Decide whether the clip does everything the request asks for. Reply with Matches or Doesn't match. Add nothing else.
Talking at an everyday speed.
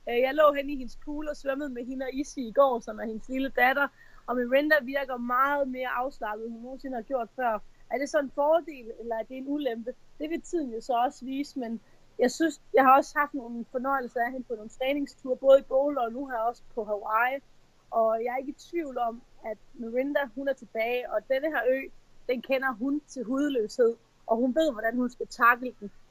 Doesn't match